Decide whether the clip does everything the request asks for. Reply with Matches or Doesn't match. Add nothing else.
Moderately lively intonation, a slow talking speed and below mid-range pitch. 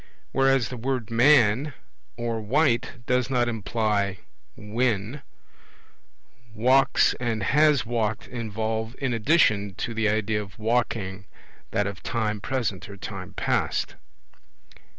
Matches